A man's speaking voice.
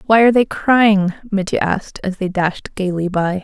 No: female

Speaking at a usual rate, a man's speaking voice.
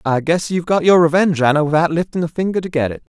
No: fast, 265 wpm; male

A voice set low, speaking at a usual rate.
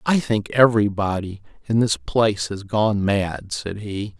Yes: low, 105 Hz; average, 155 wpm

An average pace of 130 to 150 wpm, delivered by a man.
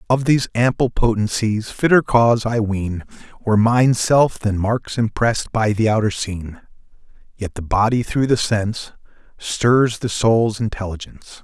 Yes: average, 145 wpm; male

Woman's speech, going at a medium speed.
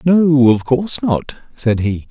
No: male; average, 170 wpm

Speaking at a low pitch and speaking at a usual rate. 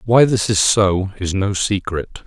Yes: low, 100 Hz; average, 185 wpm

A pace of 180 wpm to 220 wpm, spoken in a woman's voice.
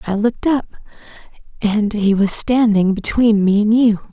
No: average, 160 wpm; female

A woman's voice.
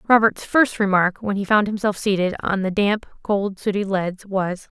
Yes: female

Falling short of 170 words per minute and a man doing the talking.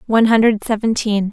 No: slow, 135 wpm; female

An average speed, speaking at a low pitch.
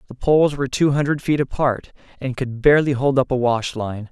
No: fast, 220 wpm; low, 130 Hz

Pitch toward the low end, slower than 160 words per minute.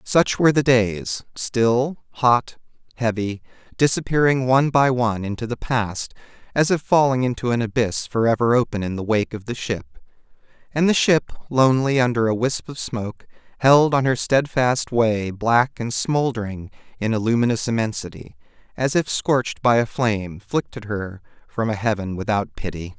No: low, 120 Hz; average, 165 wpm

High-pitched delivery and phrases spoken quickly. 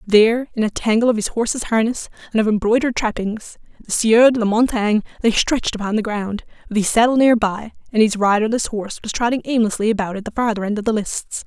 Yes: high, 220 Hz; fast, 220 wpm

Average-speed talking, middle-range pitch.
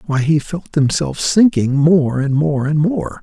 Yes: average, 185 wpm; medium, 145 Hz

